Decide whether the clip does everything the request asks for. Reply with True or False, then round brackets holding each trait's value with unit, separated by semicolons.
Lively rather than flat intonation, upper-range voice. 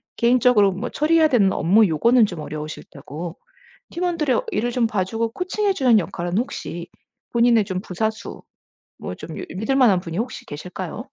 True (5.8 semitones; 220 Hz)